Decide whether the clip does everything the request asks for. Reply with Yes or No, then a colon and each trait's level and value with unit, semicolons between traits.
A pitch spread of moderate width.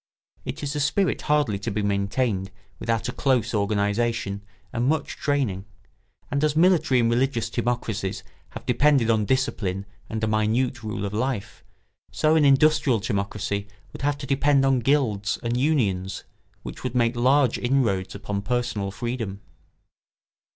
Yes: average, 4.9 semitones